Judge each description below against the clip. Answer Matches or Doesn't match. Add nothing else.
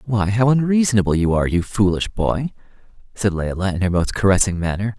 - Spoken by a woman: Doesn't match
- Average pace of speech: Matches